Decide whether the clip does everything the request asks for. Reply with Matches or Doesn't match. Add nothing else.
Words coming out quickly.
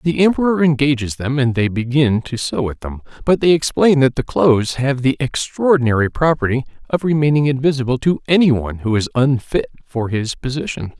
Doesn't match